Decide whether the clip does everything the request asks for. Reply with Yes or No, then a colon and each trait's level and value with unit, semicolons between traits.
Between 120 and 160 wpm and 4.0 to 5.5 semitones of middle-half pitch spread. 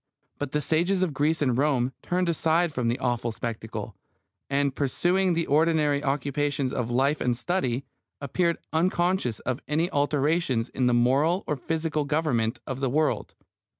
Yes: average, 155 wpm; average, 4.4 semitones